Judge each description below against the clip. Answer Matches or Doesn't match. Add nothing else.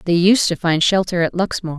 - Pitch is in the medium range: Matches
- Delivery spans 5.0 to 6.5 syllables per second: Matches